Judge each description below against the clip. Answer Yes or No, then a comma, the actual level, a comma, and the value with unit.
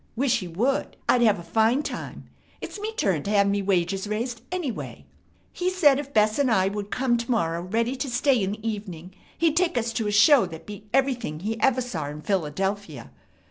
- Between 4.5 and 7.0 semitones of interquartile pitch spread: Yes, average, 5.1 semitones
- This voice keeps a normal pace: No, fast, 210 wpm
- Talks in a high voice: Yes, high, 215 Hz